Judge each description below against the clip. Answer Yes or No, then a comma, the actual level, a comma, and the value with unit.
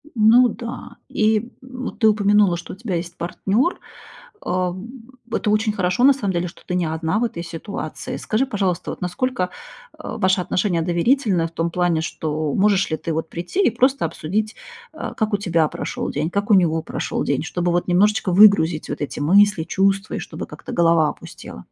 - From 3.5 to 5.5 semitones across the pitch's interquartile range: Yes, average, 4.1 semitones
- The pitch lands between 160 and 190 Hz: Yes, medium, 185 Hz